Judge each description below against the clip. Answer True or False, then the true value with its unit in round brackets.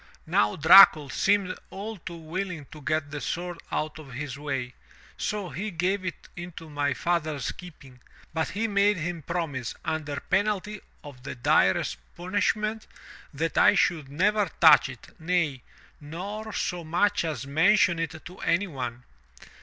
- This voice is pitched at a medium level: True (165 Hz)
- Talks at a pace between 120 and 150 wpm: True (145 wpm)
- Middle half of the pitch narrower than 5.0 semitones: True (4.6 semitones)